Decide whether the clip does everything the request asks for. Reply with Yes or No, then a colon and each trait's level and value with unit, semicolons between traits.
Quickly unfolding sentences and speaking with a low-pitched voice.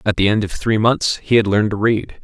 Yes: fast, 295 wpm; low, 110 Hz